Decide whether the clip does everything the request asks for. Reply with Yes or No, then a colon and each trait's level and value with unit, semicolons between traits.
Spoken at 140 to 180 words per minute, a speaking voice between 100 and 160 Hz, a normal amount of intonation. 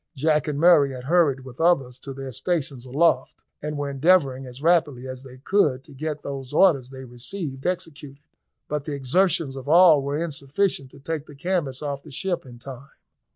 No: average, 190 wpm; medium, 140 Hz; average, 3.5 semitones